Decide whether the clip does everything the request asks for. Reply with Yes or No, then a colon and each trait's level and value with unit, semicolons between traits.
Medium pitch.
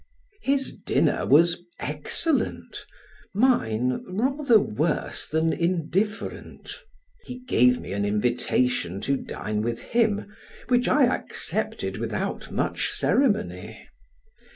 Yes: medium, 175 Hz